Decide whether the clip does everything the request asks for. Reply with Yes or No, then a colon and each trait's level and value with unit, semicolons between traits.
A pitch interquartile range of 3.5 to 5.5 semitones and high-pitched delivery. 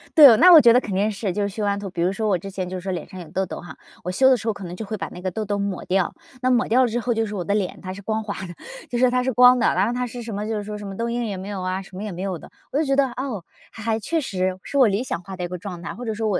Yes: average, 4.0 semitones; high, 205 Hz